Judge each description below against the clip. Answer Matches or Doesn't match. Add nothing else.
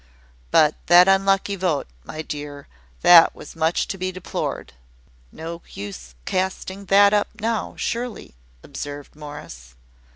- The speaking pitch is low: Doesn't match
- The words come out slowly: Matches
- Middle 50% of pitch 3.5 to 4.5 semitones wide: Doesn't match